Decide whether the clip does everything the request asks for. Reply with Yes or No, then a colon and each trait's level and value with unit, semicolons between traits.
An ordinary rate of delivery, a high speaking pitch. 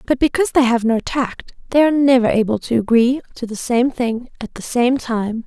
No: fast, 220 wpm; high, 245 Hz